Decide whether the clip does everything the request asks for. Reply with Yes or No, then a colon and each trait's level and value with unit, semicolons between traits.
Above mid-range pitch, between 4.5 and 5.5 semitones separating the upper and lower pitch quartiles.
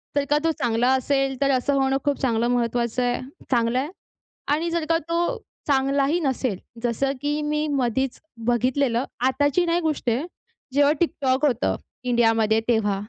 No: very high, 265 Hz; average, 3.2 semitones